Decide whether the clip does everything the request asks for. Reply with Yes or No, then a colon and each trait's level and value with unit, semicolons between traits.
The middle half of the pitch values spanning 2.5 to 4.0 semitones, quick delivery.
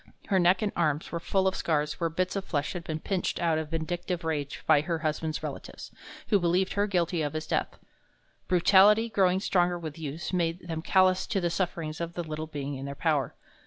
Yes: average, 2.8 semitones; fast, 210 wpm